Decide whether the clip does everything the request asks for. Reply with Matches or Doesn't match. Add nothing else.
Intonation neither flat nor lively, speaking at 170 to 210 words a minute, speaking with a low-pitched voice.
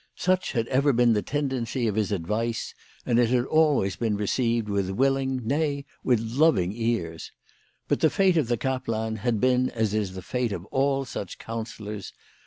Matches